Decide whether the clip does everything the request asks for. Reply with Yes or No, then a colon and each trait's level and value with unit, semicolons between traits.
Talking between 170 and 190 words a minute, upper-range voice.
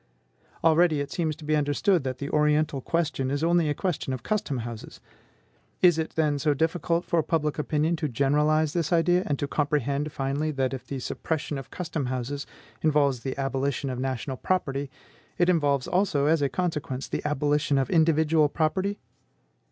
No: average, 175 wpm; medium, 150 Hz